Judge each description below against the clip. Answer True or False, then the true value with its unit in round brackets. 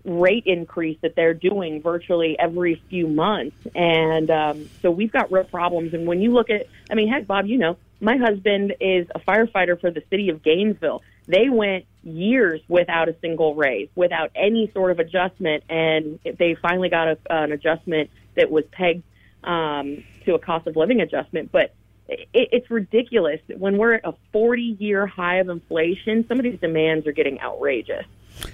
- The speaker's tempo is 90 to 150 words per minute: False (180 wpm)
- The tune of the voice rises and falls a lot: False (4.2 semitones)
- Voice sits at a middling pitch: True (175 Hz)